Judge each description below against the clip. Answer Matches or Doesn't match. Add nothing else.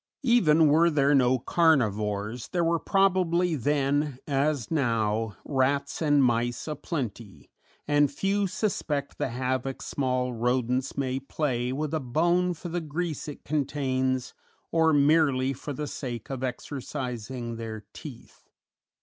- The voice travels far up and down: Doesn't match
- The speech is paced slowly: Matches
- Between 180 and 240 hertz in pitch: Doesn't match